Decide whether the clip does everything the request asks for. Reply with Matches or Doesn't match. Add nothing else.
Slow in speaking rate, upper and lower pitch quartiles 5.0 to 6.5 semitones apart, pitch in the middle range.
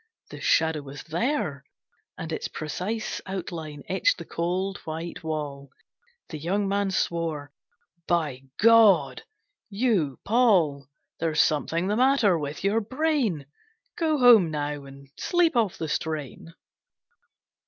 Matches